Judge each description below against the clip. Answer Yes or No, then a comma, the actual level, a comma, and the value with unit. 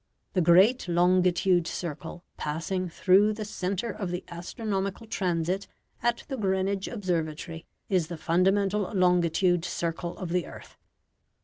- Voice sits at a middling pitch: Yes, medium, 180 Hz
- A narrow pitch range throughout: Yes, narrow, 2.3 semitones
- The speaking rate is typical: No, slow, 125 wpm